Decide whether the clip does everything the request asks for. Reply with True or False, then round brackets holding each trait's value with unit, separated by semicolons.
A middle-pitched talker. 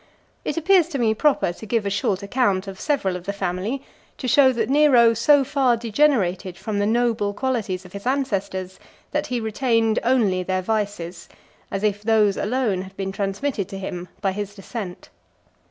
False (210 Hz)